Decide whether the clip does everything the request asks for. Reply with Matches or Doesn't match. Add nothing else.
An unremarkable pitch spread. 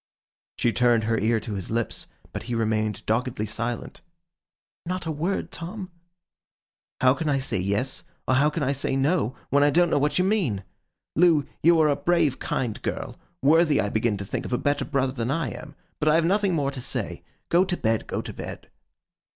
Doesn't match